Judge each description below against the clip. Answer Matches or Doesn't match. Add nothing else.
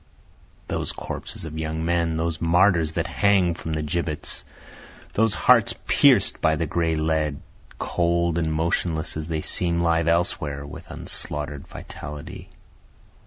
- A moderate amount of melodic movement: Doesn't match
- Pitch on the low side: Matches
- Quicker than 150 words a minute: Doesn't match